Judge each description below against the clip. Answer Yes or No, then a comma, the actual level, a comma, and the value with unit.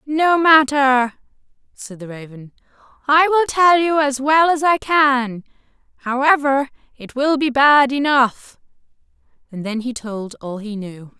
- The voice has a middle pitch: No, very high, 265 Hz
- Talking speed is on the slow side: No, average, 145 wpm